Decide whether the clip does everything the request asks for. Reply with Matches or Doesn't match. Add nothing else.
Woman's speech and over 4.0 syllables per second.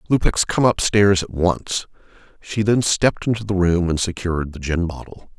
Doesn't match